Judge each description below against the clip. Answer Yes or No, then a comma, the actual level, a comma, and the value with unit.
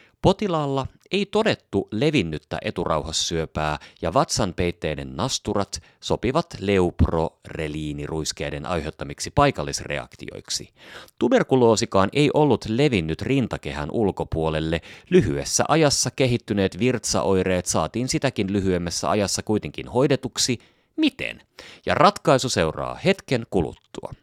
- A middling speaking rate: No, slow, 85 wpm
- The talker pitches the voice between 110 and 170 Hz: No, low, 100 Hz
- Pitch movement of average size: No, wide, 8.5 semitones